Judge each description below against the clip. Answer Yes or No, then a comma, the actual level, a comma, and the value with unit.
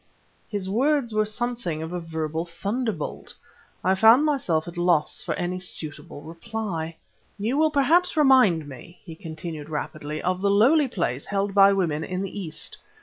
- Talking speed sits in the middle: Yes, average, 160 wpm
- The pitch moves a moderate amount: No, wide, 5.8 semitones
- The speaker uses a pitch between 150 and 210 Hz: Yes, medium, 185 Hz